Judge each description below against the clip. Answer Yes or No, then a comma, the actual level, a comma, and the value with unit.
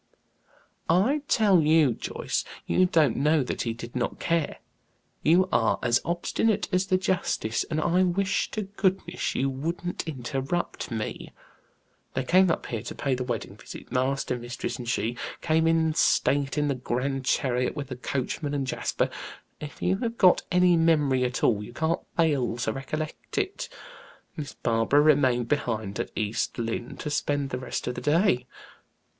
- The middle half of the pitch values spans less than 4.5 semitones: No, average, 5.3 semitones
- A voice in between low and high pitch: Yes, medium, 145 Hz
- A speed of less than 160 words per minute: No, average, 165 wpm